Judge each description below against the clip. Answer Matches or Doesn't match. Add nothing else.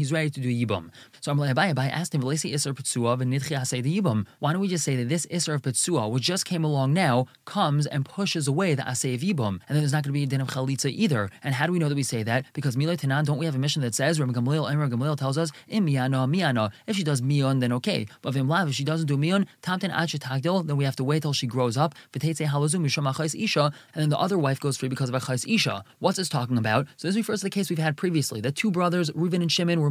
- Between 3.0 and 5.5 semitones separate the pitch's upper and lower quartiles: Matches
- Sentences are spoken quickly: Matches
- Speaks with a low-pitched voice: Doesn't match